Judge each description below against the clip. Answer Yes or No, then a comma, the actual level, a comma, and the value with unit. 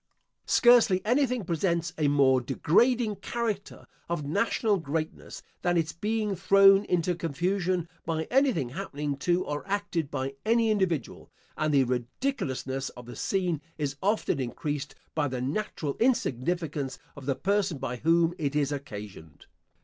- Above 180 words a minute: No, average, 140 wpm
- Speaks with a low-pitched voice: No, medium, 165 Hz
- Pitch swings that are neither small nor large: No, wide, 6.0 semitones